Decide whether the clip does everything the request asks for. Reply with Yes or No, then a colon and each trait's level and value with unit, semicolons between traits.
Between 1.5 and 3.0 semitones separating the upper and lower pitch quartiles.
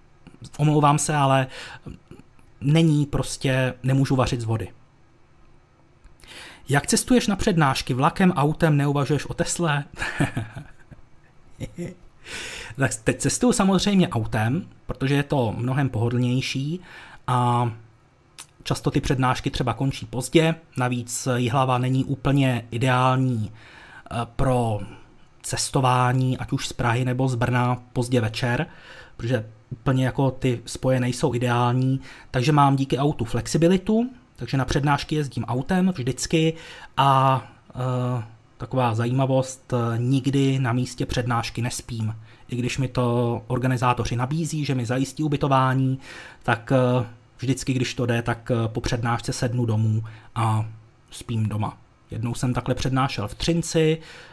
Yes: average, 2.7 semitones